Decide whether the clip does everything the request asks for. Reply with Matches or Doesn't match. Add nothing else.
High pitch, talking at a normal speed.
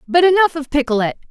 Matches